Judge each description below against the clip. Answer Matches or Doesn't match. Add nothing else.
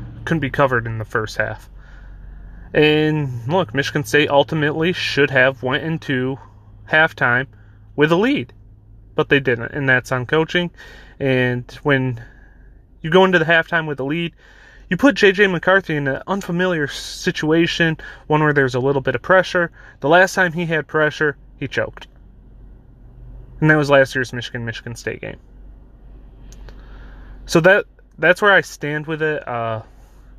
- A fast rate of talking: Doesn't match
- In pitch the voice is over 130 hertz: Matches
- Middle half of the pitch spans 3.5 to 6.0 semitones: Matches